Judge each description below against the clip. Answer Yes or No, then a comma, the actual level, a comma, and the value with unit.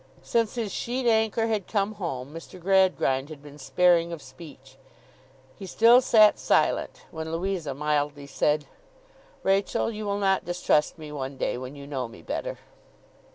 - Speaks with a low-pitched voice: No, medium, 170 Hz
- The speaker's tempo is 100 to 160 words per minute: Yes, average, 155 wpm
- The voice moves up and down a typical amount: No, wide, 6.0 semitones